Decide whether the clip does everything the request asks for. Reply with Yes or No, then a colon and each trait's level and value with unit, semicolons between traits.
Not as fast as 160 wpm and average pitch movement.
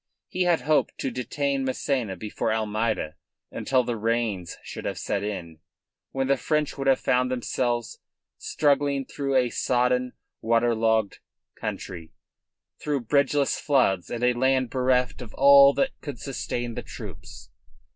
Yes: average, 145 wpm; average, 3.3 semitones